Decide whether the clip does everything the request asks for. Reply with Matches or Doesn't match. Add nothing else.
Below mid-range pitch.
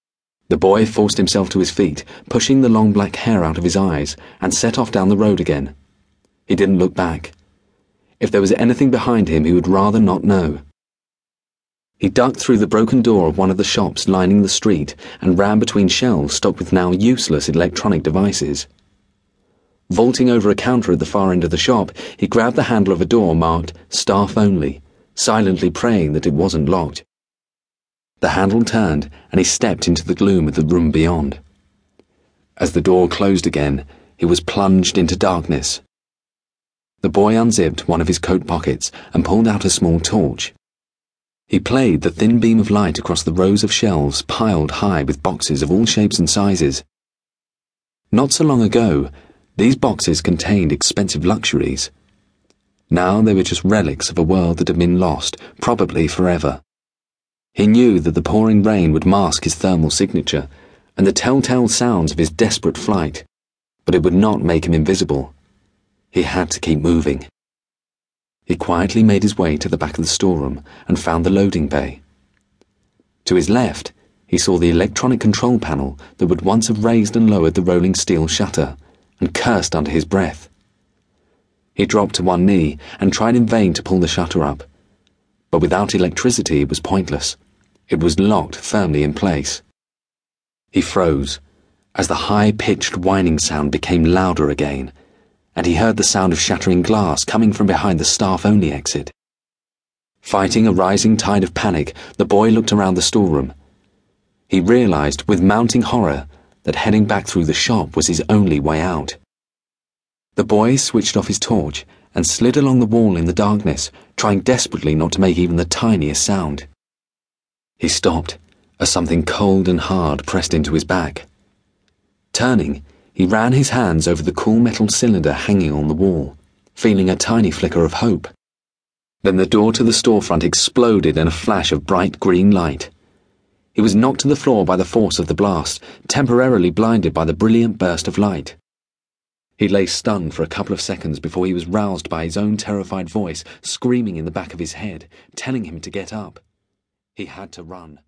Matches